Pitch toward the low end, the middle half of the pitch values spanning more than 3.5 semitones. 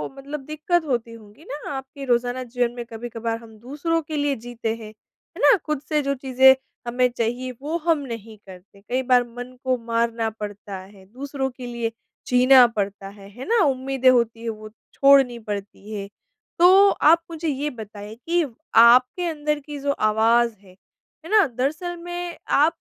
No: very high, 250 Hz; average, 4.2 semitones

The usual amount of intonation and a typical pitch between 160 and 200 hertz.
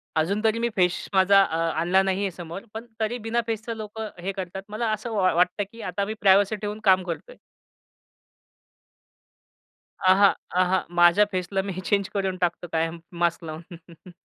Yes: average, 3.0 semitones; high, 190 Hz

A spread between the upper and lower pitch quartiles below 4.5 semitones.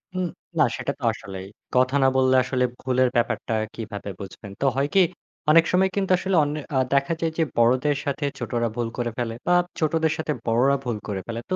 No: average, 5.0 semitones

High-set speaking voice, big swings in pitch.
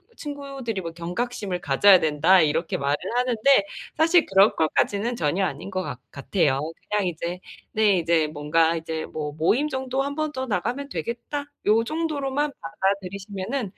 Yes: high, 200 Hz; wide, 8.0 semitones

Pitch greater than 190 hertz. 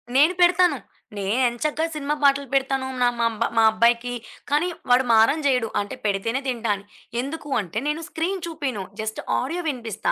Yes: very high, 260 Hz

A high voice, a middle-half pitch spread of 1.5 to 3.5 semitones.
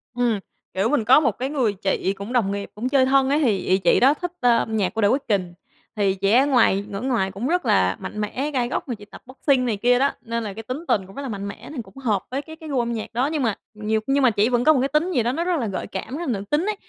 No: high, 240 Hz; average, 4.9 semitones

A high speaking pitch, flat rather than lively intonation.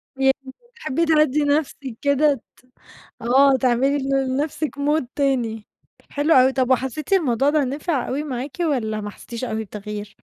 No: very high, 270 Hz; average, 3.1 semitones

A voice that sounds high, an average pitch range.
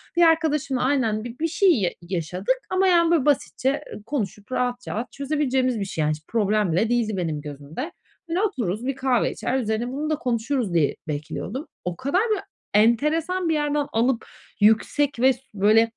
No: very high, 250 Hz; wide, 5.8 semitones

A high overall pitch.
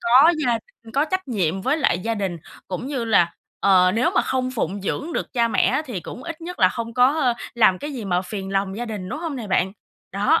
Yes: high, 230 Hz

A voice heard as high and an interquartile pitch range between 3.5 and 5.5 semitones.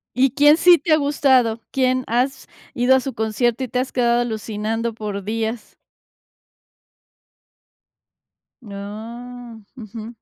No: high, 240 Hz; average, 2.8 semitones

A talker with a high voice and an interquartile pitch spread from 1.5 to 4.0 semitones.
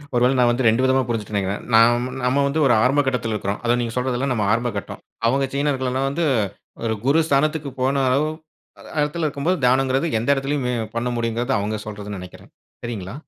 No: low, 125 Hz; average, 3.2 semitones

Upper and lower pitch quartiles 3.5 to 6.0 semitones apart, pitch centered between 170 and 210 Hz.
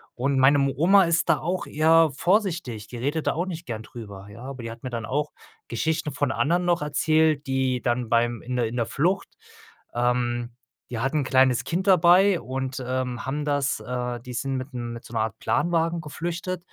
No: average, 5.1 semitones; low, 135 Hz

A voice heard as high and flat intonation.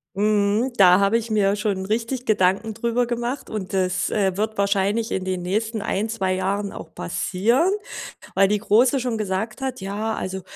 No: high, 210 Hz; average, 3.0 semitones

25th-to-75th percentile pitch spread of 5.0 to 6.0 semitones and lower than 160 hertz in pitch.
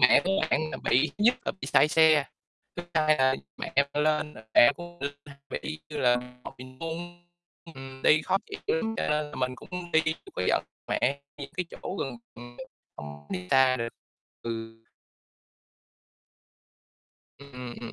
No: average, 3.9 semitones; medium, 140 Hz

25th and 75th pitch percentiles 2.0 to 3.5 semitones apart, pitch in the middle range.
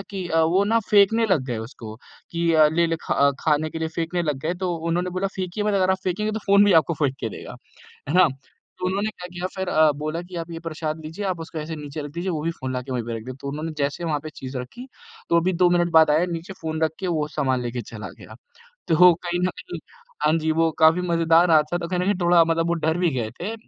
Yes: average, 2.9 semitones; medium, 165 Hz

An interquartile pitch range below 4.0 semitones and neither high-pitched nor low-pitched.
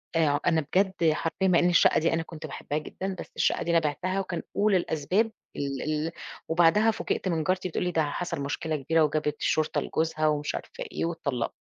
Yes: average, 2.9 semitones; medium, 165 Hz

